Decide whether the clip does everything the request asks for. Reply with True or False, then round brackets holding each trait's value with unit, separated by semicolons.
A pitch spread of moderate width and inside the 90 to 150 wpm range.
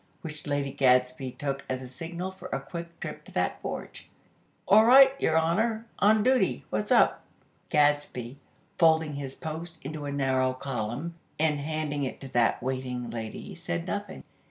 False (4.1 semitones; 160 wpm)